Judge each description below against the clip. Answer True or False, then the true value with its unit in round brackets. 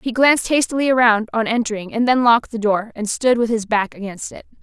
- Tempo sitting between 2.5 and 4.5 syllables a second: False (5.9 syllables/s)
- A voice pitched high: True (230 Hz)